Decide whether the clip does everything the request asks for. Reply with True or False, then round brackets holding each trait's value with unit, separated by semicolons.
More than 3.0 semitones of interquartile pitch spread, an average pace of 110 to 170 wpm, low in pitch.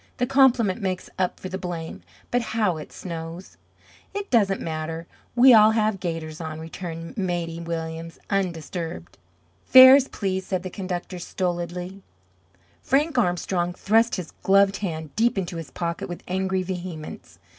False (3.4 semitones; 145 wpm; 185 Hz)